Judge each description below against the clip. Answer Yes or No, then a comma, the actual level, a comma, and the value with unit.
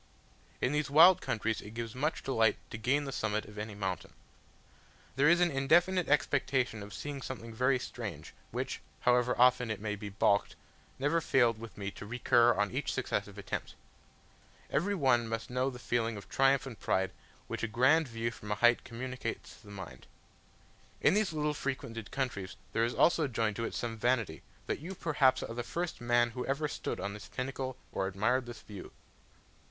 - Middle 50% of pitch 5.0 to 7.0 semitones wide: No, average, 3.7 semitones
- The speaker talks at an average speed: Yes, average, 190 wpm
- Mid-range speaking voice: No, low, 120 Hz